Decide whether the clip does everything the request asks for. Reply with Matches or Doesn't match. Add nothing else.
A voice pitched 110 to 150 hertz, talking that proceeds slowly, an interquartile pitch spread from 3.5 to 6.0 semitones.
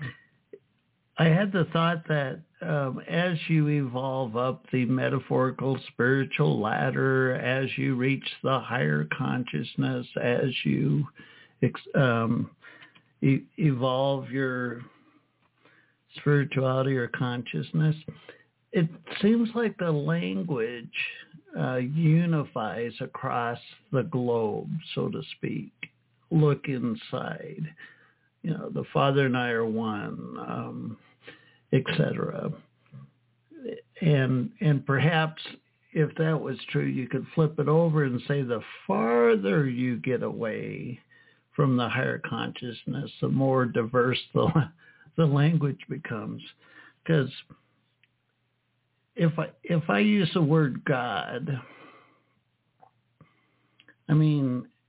Matches